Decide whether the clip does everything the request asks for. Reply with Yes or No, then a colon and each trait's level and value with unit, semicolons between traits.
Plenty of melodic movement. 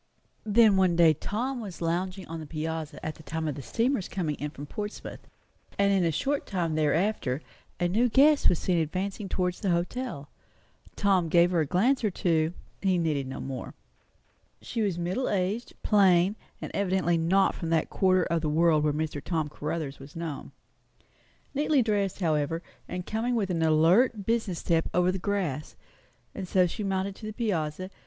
No: average, 4.0 semitones